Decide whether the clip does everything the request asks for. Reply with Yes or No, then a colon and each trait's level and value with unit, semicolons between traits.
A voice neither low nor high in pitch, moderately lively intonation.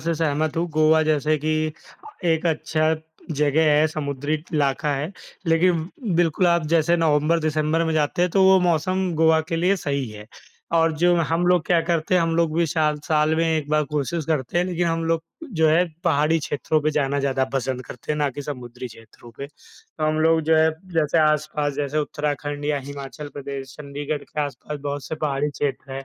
No: medium, 155 Hz; narrow, 2.2 semitones